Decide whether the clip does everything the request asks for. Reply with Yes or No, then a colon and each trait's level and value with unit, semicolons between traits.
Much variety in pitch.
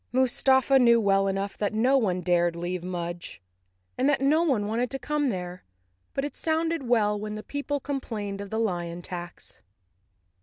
Yes: wide, 6.7 semitones